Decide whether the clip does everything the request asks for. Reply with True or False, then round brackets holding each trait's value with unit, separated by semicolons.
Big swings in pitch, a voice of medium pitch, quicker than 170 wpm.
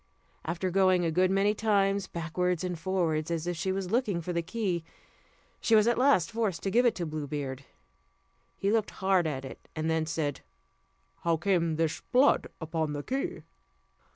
False (3.7 semitones; 180 Hz; 180 wpm)